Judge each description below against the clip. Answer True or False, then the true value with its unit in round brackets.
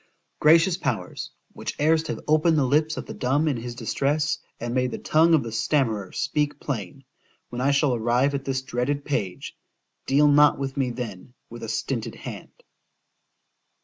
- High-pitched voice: False (135 Hz)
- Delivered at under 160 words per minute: False (170 wpm)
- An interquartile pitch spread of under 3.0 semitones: False (3.6 semitones)